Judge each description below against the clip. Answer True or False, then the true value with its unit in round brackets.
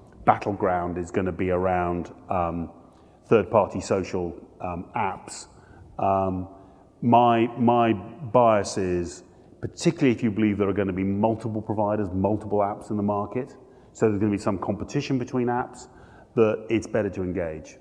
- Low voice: True (105 Hz)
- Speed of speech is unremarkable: True (160 wpm)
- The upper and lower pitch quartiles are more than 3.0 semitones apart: True (3.5 semitones)